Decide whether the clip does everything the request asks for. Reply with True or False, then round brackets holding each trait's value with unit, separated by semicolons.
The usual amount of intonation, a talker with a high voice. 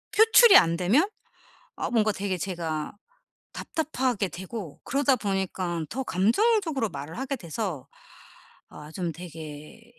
False (7.7 semitones; 195 Hz)